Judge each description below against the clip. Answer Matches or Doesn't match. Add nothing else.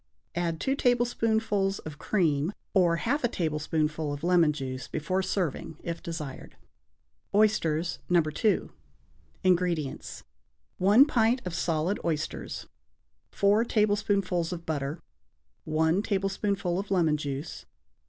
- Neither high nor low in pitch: Matches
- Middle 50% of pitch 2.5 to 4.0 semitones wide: Doesn't match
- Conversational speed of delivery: Doesn't match